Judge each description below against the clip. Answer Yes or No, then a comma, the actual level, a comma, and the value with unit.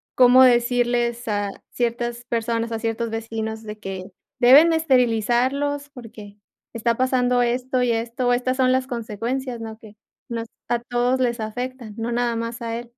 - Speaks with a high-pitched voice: Yes, high, 240 Hz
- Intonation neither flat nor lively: No, narrow, 1.8 semitones